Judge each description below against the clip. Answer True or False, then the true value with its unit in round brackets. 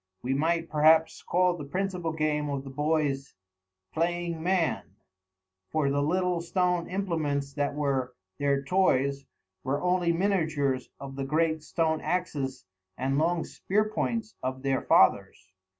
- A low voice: False (155 Hz)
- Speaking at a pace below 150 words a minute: True (135 wpm)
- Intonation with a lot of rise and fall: False (4.0 semitones)